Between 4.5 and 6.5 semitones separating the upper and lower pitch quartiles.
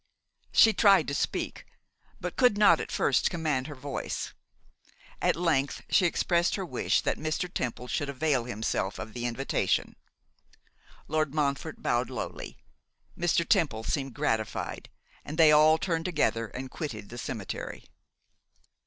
Yes: average, 4.9 semitones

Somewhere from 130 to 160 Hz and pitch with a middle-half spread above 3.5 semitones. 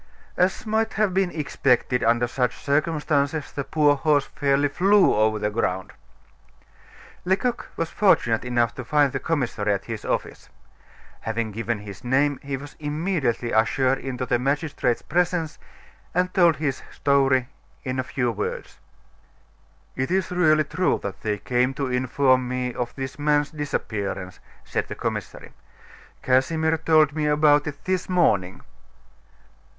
Yes: medium, 140 Hz; average, 4.4 semitones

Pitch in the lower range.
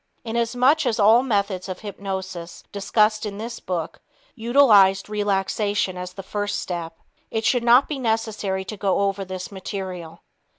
No: high, 205 Hz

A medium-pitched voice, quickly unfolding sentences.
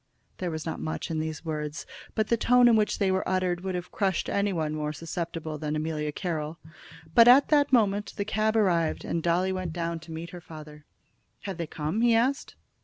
Yes: medium, 175 Hz; fast, 210 wpm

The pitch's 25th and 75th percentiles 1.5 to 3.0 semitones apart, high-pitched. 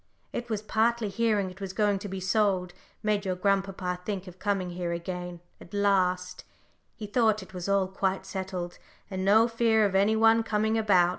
Yes: narrow, 2.6 semitones; high, 195 Hz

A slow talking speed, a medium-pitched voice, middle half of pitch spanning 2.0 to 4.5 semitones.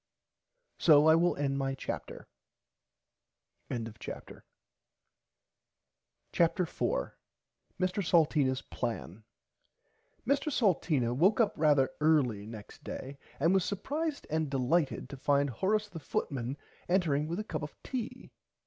No: slow, 120 wpm; medium, 155 Hz; wide, 5.4 semitones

